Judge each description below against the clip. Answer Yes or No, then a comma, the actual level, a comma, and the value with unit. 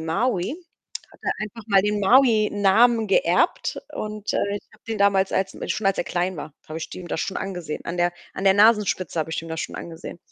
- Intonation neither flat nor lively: Yes, average, 3.4 semitones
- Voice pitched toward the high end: Yes, high, 195 Hz